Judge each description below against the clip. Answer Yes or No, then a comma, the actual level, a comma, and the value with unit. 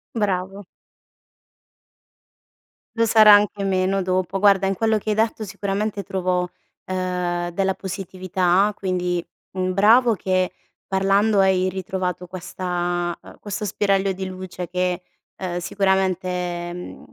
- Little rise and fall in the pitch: Yes, narrow, 1.6 semitones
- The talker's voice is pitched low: No, high, 190 Hz